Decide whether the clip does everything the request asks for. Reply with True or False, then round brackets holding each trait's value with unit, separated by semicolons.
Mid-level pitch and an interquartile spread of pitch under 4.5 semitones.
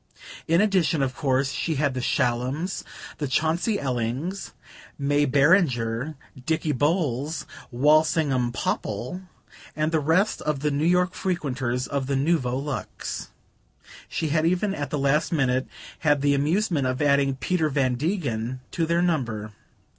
True (145 Hz; 3.9 semitones)